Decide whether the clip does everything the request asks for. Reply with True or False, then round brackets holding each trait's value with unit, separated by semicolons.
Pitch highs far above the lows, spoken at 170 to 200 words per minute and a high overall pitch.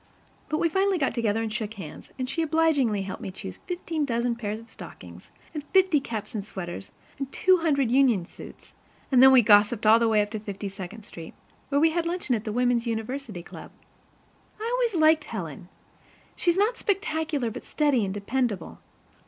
True (6.7 semitones; 190 wpm; 245 Hz)